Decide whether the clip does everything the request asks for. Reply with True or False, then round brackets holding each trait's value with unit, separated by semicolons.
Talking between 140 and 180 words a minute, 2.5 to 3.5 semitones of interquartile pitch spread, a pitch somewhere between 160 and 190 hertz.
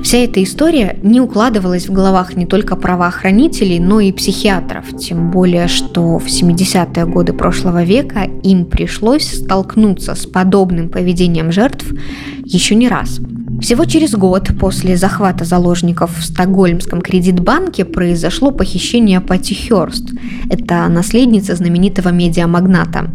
False (125 wpm; 3.0 semitones; 185 Hz)